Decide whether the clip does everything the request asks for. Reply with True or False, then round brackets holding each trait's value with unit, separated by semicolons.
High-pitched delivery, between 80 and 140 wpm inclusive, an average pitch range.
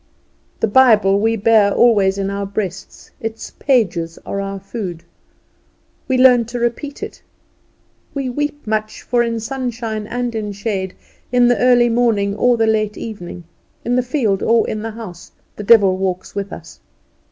False (220 Hz; 165 wpm; 3.4 semitones)